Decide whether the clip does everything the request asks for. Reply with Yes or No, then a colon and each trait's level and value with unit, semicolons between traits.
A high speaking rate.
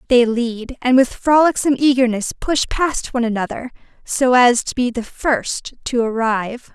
No: average, 160 wpm